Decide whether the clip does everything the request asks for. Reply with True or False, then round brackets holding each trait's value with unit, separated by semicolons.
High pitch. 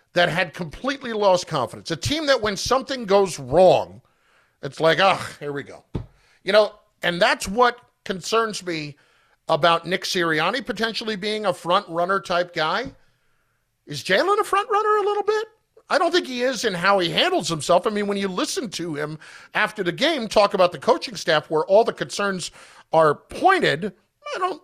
True (195 Hz)